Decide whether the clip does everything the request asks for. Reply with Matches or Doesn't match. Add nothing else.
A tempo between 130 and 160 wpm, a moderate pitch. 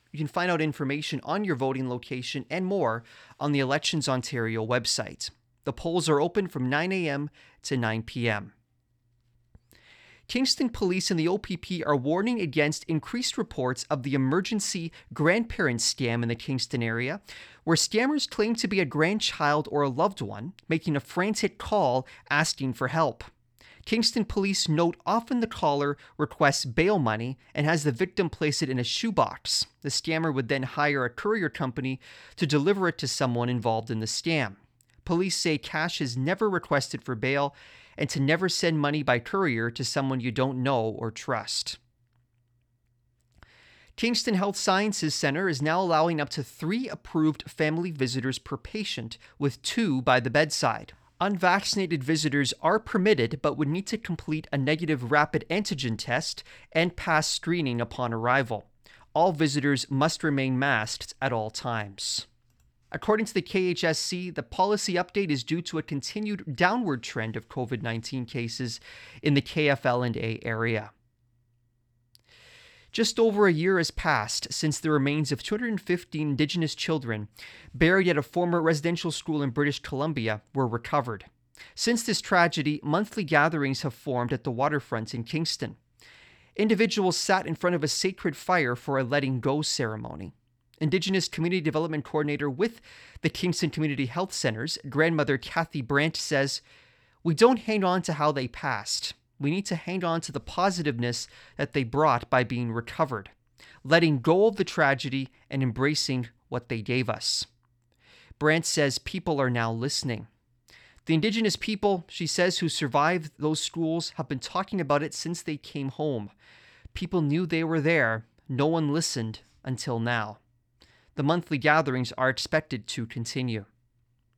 Matches